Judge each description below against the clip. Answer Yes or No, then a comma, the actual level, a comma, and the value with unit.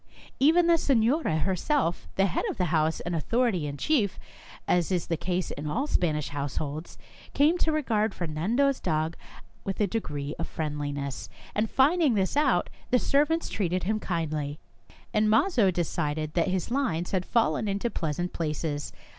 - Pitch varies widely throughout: Yes, wide, 7.3 semitones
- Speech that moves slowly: No, average, 165 wpm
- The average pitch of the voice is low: No, medium, 185 Hz